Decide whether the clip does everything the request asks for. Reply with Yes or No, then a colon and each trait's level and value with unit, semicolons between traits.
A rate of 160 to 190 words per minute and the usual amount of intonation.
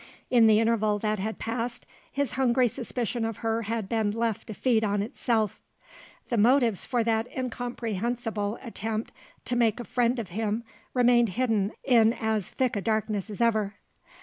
No: average, 165 wpm; narrow, 2.1 semitones